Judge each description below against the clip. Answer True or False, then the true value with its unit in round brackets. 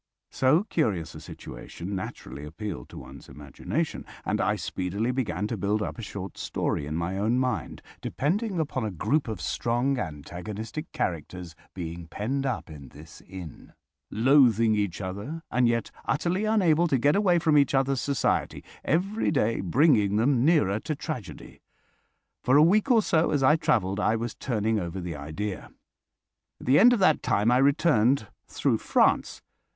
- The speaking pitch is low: True (115 Hz)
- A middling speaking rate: True (165 wpm)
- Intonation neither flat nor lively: False (7.7 semitones)